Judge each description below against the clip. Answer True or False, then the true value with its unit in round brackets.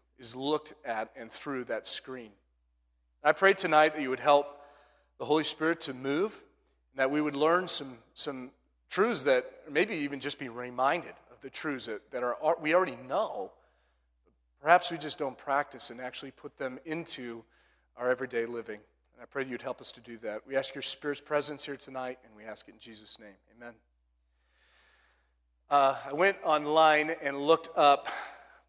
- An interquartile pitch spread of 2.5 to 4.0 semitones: False (4.5 semitones)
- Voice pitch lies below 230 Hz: True (135 Hz)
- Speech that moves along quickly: False (185 wpm)